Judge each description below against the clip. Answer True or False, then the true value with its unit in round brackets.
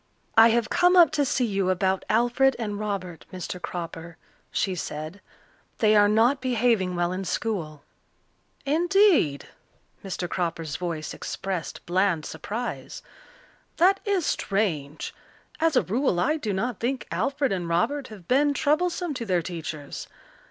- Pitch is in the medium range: False (205 Hz)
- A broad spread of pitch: True (7.2 semitones)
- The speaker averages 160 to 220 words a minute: False (140 wpm)